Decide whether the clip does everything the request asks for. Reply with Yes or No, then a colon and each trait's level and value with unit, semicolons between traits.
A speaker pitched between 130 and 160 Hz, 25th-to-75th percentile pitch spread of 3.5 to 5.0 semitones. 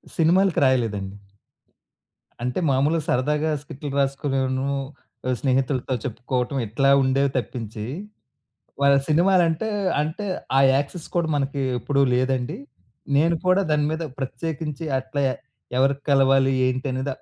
No: low, 135 Hz; average, 2.8 semitones